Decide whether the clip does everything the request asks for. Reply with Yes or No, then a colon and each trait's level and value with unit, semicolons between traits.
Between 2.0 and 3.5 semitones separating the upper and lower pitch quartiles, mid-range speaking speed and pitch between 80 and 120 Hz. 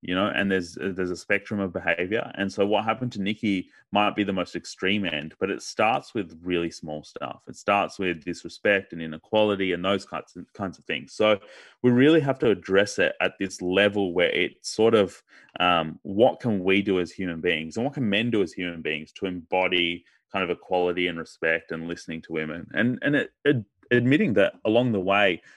No: average, 2.8 semitones; fast, 210 wpm; very low, 95 Hz